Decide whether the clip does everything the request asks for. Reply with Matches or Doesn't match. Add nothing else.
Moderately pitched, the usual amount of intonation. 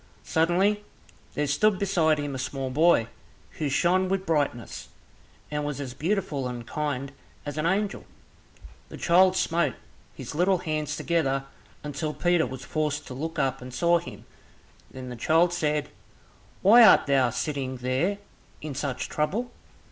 Matches